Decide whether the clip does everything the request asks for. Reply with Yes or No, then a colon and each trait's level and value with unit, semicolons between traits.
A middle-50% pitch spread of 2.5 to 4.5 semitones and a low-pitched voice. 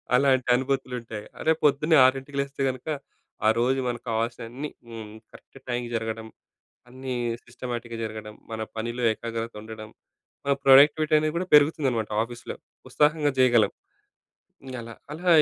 Yes: average, 3.4 semitones; low, 125 Hz